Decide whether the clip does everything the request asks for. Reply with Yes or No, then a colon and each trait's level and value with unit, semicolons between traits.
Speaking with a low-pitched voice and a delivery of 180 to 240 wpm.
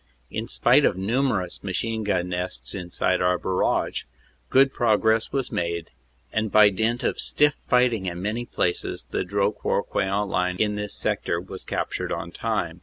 No: low, 100 Hz; average, 165 wpm